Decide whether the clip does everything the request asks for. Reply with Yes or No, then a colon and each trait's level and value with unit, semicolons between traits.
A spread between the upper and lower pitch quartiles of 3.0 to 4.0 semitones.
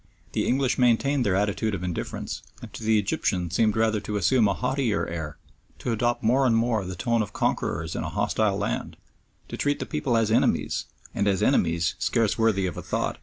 Yes: average, 3.6 semitones